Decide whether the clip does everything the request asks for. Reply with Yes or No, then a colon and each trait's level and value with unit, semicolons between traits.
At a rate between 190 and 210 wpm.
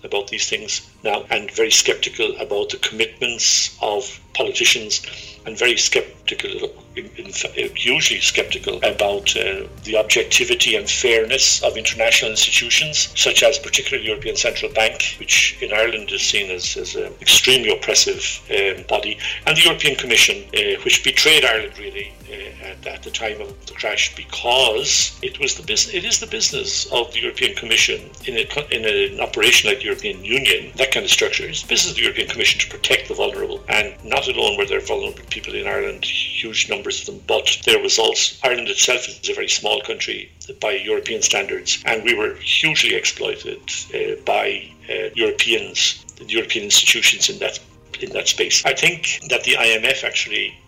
No: average, 175 wpm